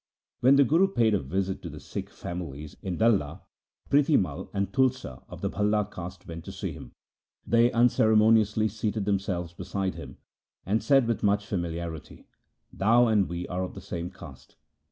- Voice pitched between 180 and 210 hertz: No, low, 100 Hz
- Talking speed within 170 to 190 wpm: Yes, average, 180 wpm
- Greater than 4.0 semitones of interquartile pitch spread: Yes, average, 4.4 semitones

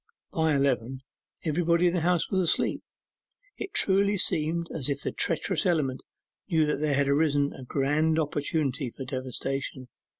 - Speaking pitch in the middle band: Yes, medium, 150 Hz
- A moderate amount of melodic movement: Yes, average, 3.6 semitones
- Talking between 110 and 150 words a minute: Yes, average, 145 wpm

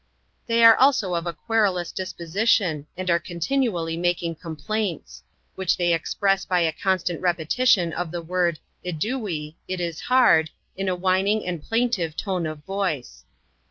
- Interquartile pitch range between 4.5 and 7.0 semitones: No, average, 3.3 semitones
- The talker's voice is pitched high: No, medium, 180 Hz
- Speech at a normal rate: Yes, average, 155 wpm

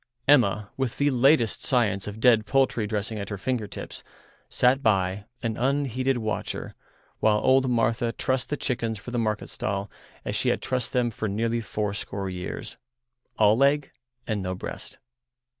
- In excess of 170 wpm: No, average, 160 wpm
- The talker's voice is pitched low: Yes, low, 115 Hz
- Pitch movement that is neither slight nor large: Yes, average, 3.4 semitones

